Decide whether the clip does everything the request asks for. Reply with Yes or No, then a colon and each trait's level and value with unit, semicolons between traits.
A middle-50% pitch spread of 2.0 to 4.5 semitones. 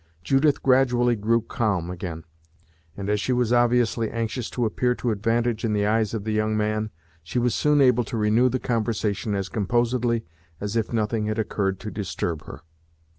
Yes: average, 2.7 semitones